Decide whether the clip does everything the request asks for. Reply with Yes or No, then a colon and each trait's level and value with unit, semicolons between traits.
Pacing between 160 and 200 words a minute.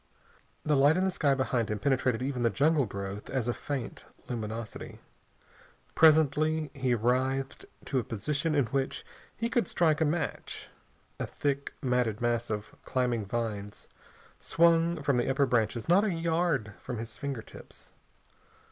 No: average, 150 wpm